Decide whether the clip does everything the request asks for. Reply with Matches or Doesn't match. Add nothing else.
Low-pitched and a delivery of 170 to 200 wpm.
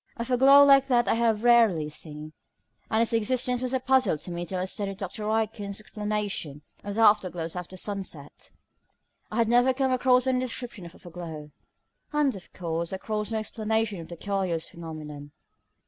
Doesn't match